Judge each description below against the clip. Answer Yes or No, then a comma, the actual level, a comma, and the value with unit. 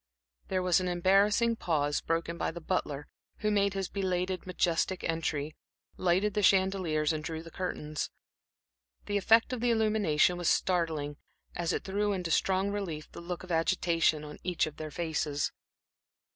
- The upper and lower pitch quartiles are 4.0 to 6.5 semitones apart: No, average, 3.3 semitones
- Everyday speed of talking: Yes, average, 160 wpm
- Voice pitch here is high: No, medium, 180 Hz